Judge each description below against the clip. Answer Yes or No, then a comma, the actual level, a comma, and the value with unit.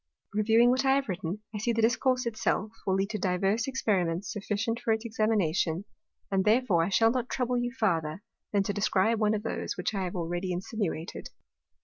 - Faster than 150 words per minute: Yes, average, 200 wpm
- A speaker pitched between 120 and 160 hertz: No, high, 210 Hz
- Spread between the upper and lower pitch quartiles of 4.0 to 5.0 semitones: No, average, 3.6 semitones